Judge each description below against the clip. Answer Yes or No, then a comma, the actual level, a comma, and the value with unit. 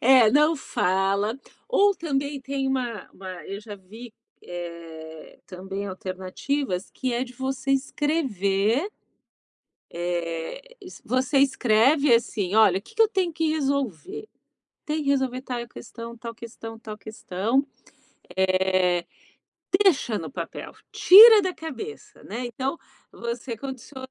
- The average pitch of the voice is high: Yes, high, 240 Hz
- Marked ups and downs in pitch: Yes, wide, 6.1 semitones